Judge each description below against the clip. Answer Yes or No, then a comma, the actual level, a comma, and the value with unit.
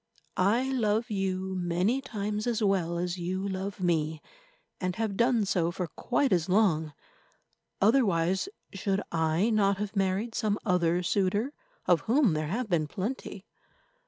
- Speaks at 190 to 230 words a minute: No, average, 145 wpm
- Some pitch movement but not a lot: Yes, average, 3.6 semitones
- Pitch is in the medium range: No, high, 195 Hz